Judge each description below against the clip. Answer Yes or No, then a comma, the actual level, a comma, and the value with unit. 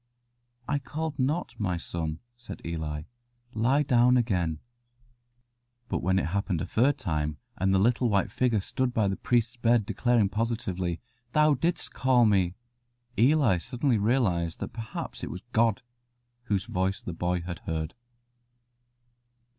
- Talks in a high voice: No, low, 110 Hz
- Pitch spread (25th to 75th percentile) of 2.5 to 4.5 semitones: No, wide, 5.6 semitones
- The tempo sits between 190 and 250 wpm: No, average, 145 wpm